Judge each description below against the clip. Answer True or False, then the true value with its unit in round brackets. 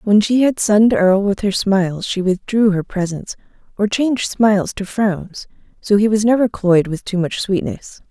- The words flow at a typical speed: True (190 wpm)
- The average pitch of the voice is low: False (205 Hz)